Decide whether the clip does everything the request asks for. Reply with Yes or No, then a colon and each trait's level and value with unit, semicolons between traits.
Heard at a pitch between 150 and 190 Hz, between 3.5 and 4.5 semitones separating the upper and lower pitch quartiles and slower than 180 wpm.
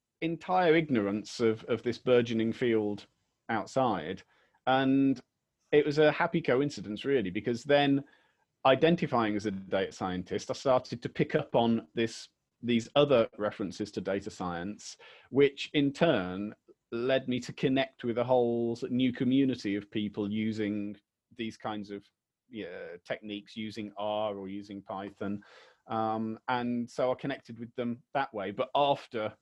No: low, 120 Hz; average, 4.2 semitones; average, 145 wpm